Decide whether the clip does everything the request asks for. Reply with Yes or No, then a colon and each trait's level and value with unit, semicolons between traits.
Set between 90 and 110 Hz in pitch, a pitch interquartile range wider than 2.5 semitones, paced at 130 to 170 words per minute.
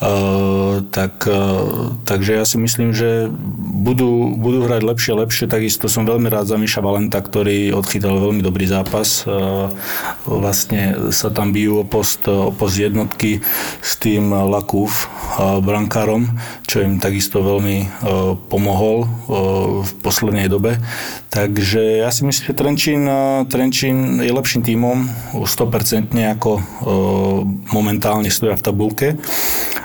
Yes: low, 105 Hz; average, 2.9 semitones; average, 135 wpm